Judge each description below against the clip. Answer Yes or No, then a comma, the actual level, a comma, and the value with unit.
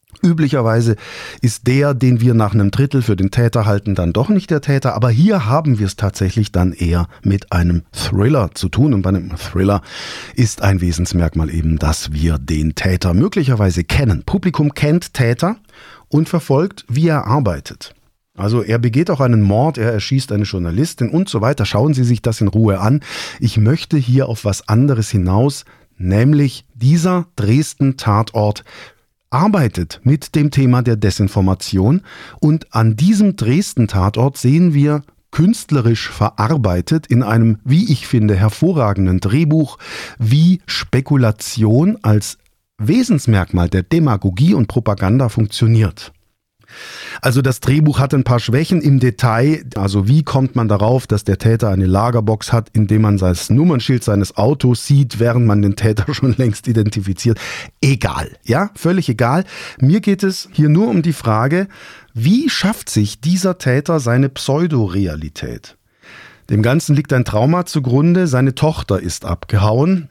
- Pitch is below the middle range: Yes, low, 120 Hz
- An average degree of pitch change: No, wide, 6.1 semitones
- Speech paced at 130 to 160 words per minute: Yes, average, 150 wpm